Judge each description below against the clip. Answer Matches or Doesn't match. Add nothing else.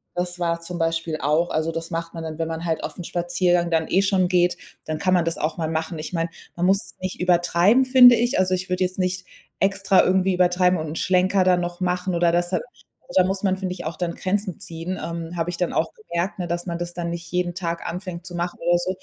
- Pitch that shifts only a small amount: Matches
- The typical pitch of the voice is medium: Matches